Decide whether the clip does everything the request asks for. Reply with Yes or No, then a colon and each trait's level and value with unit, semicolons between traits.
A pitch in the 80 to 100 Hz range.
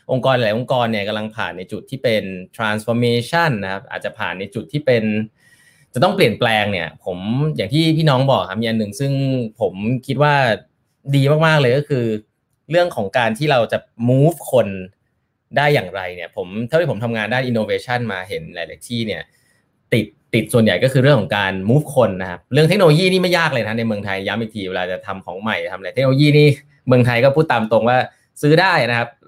No: low, 120 Hz